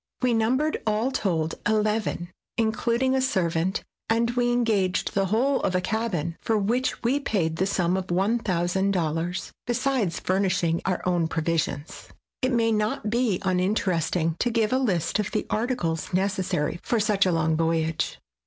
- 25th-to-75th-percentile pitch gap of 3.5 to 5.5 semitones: Yes, average, 5.0 semitones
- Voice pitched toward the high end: Yes, high, 195 Hz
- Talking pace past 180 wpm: No, average, 155 wpm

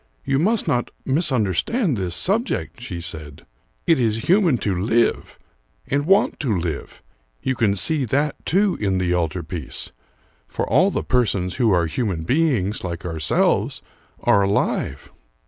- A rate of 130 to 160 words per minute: Yes, average, 145 wpm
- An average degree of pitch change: No, wide, 8.4 semitones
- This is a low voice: Yes, low, 110 Hz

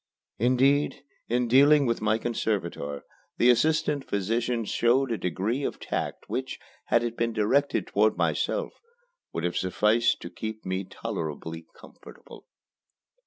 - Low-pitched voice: Yes, low, 115 Hz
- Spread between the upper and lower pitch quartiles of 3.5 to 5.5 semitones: Yes, average, 4.2 semitones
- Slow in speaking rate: Yes, slow, 130 wpm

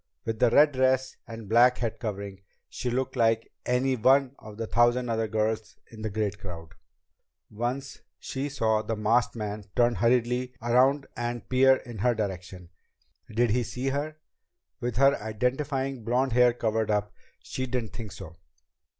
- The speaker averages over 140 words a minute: Yes, average, 160 wpm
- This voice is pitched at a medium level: No, low, 120 Hz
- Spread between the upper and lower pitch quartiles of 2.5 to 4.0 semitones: Yes, average, 2.9 semitones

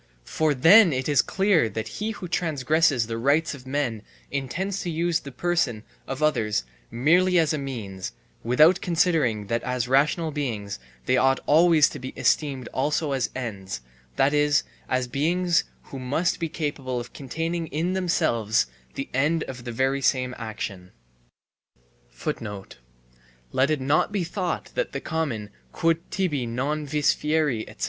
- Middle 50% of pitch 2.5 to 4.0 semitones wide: No, average, 4.7 semitones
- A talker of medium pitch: Yes, medium, 145 Hz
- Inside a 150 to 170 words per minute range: Yes, average, 155 wpm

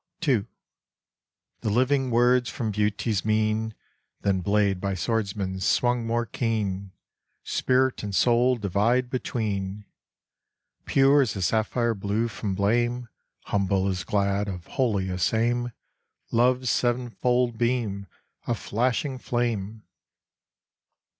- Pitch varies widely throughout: No, average, 3.5 semitones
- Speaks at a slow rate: Yes, slow, 110 wpm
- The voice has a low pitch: Yes, low, 110 Hz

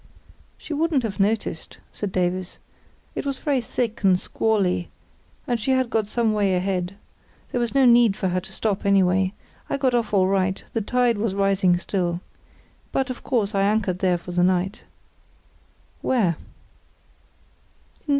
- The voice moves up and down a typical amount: Yes, average, 4.2 semitones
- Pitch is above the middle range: Yes, high, 200 Hz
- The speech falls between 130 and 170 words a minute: Yes, average, 155 wpm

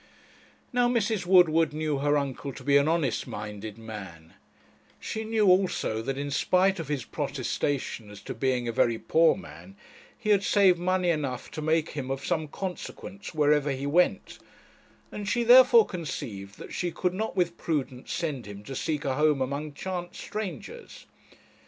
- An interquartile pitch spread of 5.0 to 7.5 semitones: Yes, wide, 5.6 semitones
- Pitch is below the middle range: No, medium, 155 Hz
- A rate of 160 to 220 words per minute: Yes, average, 170 wpm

